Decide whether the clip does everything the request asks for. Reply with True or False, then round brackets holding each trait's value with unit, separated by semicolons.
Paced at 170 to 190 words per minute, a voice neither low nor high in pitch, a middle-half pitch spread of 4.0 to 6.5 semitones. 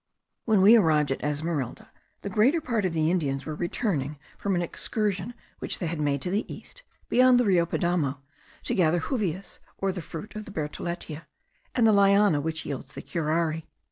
True (185 wpm; 175 Hz; 4.9 semitones)